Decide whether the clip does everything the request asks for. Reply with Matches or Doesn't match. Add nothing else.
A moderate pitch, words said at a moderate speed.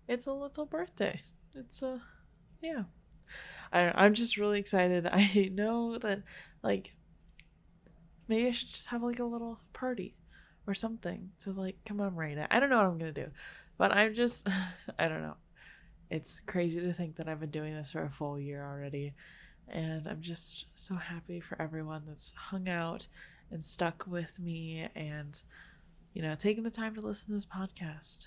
Matches